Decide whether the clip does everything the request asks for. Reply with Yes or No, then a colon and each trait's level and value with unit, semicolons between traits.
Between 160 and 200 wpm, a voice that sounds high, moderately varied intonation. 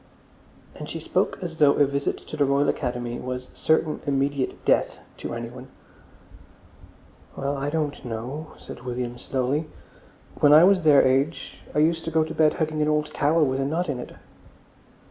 No: average, 175 wpm; medium, 145 Hz; average, 3.1 semitones